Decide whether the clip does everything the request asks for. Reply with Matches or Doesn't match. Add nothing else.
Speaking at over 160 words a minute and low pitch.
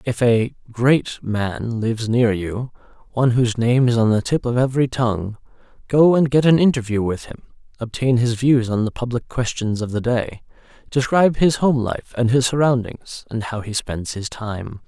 Matches